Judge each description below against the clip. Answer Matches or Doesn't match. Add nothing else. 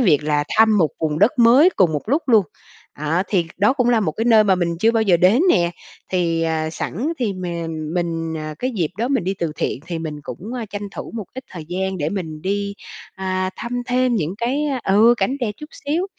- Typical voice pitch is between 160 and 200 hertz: Matches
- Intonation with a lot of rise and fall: Matches